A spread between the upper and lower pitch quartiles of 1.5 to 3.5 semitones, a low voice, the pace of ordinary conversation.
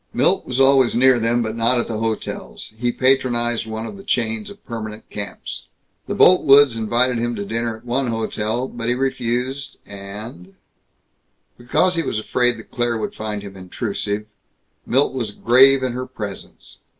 Yes: average, 2.7 semitones; low, 120 Hz; average, 170 wpm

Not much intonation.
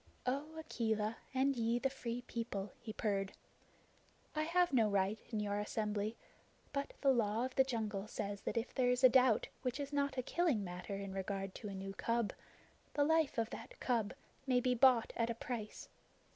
No: average, 3.9 semitones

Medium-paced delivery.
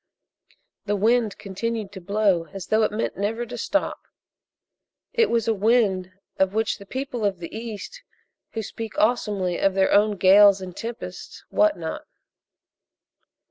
Yes: average, 150 wpm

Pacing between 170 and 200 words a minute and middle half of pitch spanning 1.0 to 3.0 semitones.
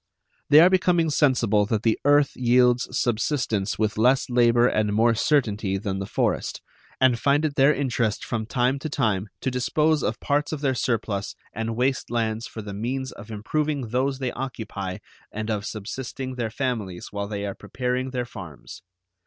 No: average, 175 wpm; average, 3.8 semitones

